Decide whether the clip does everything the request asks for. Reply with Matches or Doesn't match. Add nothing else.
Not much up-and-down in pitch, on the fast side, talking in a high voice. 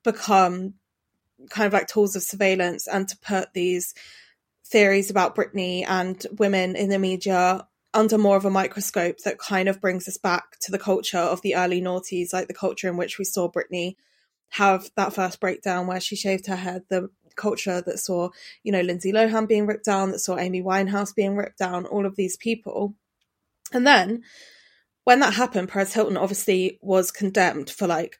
Doesn't match